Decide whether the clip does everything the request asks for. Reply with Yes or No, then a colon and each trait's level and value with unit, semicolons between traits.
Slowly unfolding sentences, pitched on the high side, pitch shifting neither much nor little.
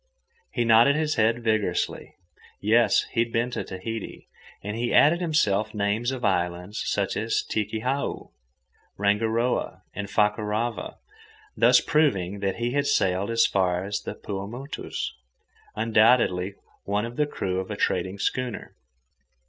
No: slow, 130 wpm; low, 110 Hz; average, 3.2 semitones